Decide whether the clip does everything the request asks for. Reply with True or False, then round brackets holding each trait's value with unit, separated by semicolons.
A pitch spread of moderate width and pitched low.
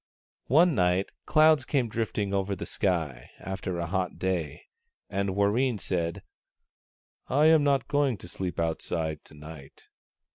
False (7.0 semitones; 95 Hz)